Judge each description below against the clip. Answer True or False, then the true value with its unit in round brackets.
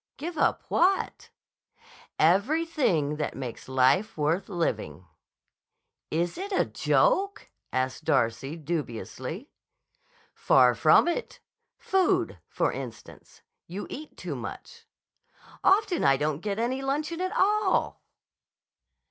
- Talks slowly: True (105 wpm)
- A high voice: True (205 Hz)